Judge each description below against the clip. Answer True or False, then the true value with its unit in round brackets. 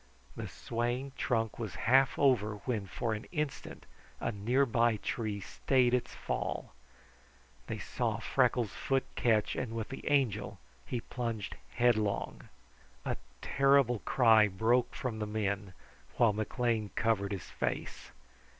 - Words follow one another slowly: True (130 wpm)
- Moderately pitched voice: False (115 Hz)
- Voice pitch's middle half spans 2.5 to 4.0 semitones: True (2.8 semitones)